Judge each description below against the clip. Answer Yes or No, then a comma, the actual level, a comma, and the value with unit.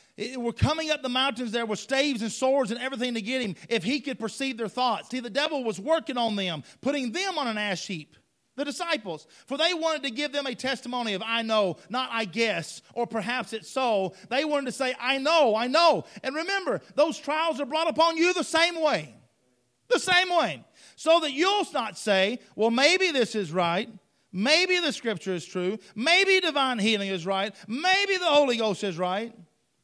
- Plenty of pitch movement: Yes, wide, 6.2 semitones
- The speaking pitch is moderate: No, very high, 250 Hz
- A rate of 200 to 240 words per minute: Yes, fast, 205 wpm